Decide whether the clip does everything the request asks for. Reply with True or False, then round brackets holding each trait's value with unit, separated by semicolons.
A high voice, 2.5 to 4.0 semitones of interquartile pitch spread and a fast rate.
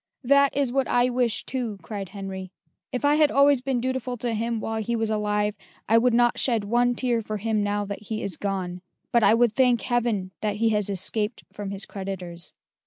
True (225 Hz; 3.1 semitones; 210 wpm)